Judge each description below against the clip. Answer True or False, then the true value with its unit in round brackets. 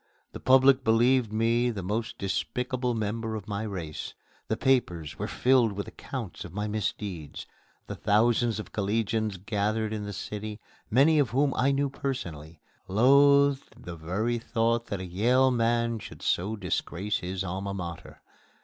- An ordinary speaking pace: True (155 wpm)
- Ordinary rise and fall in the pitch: True (3.9 semitones)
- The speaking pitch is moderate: False (110 Hz)